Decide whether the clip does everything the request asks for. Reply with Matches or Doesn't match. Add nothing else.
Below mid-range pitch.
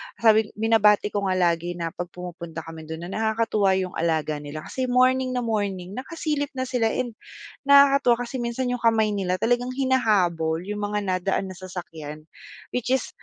Doesn't match